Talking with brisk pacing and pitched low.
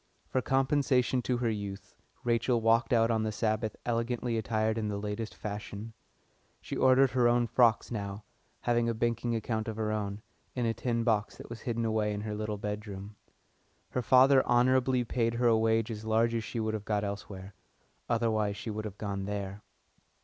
No: average, 185 wpm; low, 110 Hz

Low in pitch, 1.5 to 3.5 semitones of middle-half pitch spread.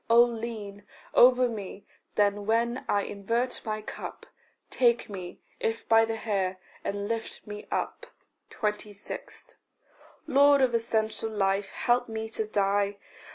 No: high, 220 Hz; narrow, 2.4 semitones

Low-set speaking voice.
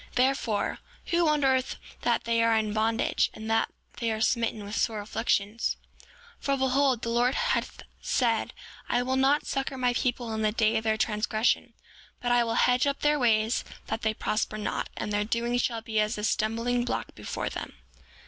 No: high, 230 Hz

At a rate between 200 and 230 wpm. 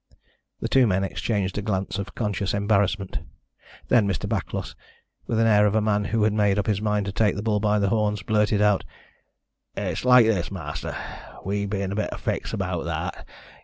Yes: fast, 205 wpm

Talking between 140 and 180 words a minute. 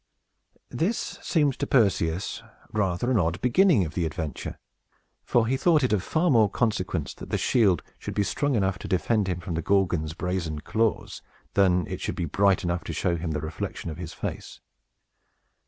No: average, 190 wpm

